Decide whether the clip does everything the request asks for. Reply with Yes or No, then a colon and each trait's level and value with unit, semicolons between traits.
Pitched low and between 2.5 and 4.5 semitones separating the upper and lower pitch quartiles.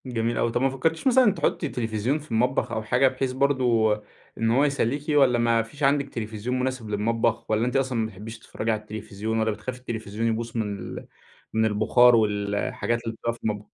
Yes: low, 115 Hz; average, 2.8 semitones